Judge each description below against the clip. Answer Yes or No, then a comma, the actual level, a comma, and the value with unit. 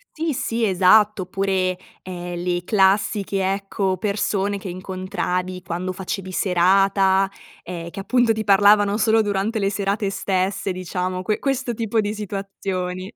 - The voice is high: Yes, high, 195 Hz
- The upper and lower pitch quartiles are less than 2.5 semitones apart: Yes, narrow, 2.0 semitones